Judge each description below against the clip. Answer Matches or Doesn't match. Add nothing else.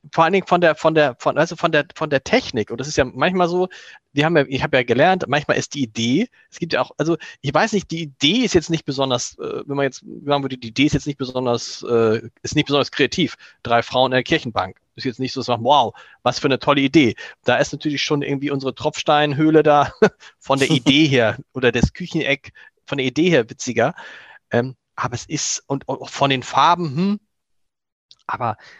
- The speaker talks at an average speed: Doesn't match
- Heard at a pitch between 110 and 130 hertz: Doesn't match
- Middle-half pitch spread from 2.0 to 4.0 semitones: Matches